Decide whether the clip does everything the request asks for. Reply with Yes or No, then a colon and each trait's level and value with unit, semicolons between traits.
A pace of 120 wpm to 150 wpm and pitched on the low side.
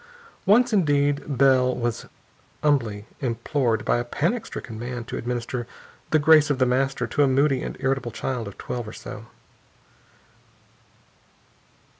Yes: average, 140 wpm; low, 130 Hz